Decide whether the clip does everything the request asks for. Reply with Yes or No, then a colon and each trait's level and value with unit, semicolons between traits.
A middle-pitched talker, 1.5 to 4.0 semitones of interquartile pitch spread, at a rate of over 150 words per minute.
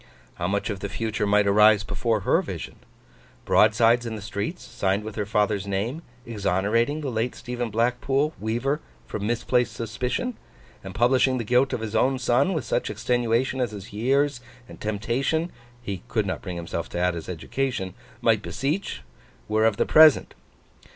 No: low, 115 Hz; average, 3.6 semitones; average, 170 wpm